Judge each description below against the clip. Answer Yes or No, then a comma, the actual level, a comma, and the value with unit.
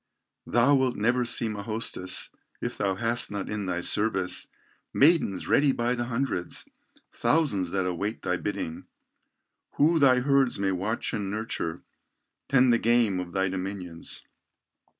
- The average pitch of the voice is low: Yes, low, 110 Hz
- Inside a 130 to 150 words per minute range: Yes, average, 145 wpm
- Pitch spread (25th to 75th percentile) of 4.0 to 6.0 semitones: Yes, average, 4.7 semitones